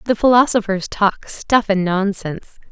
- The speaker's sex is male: No, female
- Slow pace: Yes, slow, 130 wpm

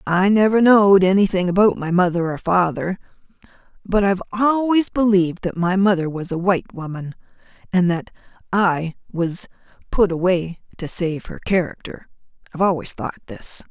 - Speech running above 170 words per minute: No, average, 160 wpm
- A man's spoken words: No, female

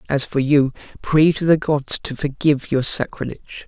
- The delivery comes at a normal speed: Yes, average, 180 wpm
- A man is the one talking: Yes, male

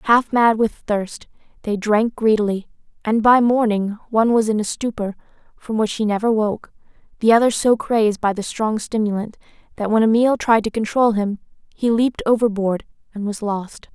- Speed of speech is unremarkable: Yes, average, 175 wpm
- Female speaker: Yes, female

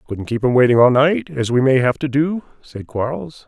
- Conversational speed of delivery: No, fast, 240 wpm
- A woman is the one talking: No, male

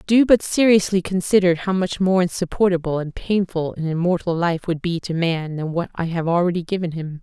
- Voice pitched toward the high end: No, medium, 175 Hz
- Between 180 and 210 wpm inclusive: Yes, average, 200 wpm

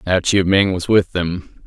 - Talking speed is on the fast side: Yes, fast, 215 wpm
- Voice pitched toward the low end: Yes, very low, 95 Hz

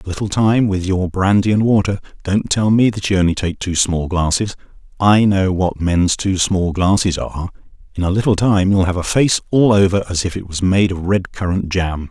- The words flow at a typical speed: No, fast, 225 wpm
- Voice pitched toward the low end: Yes, very low, 95 Hz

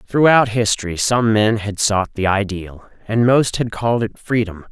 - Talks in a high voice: No, low, 110 Hz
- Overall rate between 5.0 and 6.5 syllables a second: No, 4.6 syllables/s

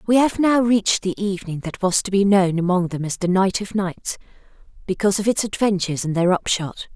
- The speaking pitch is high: Yes, high, 195 Hz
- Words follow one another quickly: Yes, fast, 215 wpm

